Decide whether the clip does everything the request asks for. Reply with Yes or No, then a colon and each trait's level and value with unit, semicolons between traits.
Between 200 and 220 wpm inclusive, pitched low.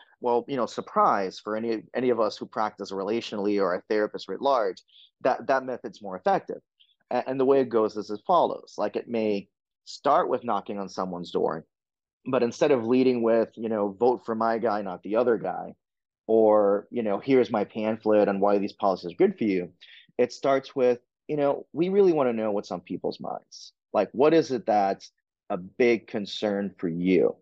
Yes: fast, 205 wpm; low, 110 Hz